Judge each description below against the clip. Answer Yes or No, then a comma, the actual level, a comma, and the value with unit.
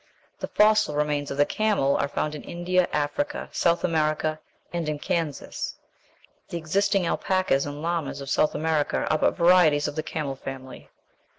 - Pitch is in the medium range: Yes, medium, 155 Hz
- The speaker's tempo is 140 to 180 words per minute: Yes, average, 165 wpm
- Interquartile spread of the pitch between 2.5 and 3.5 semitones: Yes, average, 3.2 semitones